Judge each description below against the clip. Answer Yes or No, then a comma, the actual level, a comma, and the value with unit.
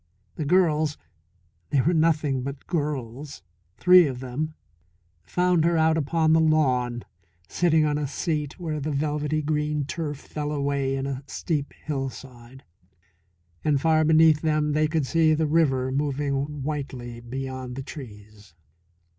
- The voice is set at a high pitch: No, medium, 150 Hz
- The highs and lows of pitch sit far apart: No, average, 2.7 semitones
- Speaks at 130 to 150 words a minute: Yes, average, 140 wpm